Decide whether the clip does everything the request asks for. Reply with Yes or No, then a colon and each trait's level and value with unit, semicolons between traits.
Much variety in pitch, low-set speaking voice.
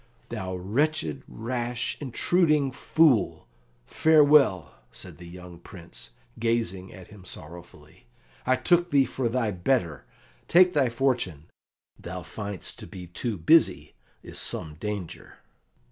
Yes: wide, 7.3 semitones; low, 115 Hz